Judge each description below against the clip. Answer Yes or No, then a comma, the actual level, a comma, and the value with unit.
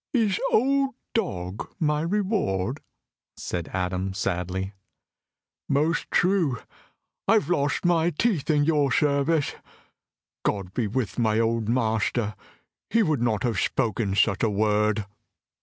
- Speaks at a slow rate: Yes, slow, 125 wpm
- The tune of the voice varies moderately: No, wide, 8.0 semitones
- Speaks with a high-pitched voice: No, low, 125 Hz